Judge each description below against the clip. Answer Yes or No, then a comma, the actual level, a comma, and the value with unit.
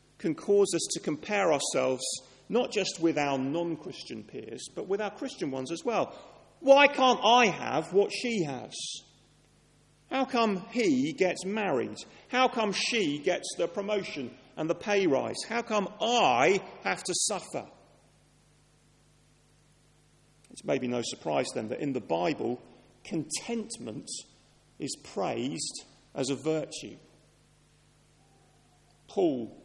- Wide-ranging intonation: Yes, wide, 7.1 semitones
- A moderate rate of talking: No, slow, 130 wpm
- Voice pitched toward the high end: Yes, high, 200 Hz